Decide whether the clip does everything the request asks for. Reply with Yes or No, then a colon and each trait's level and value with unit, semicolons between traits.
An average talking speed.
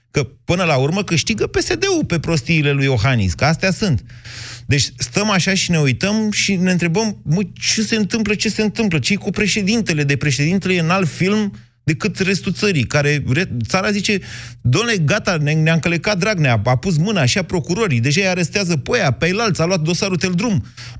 No: fast, 190 wpm